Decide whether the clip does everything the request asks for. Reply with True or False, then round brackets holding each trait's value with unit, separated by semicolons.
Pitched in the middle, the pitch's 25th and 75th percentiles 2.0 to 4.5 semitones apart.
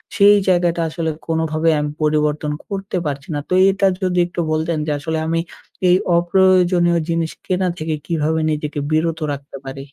True (165 Hz; 2.7 semitones)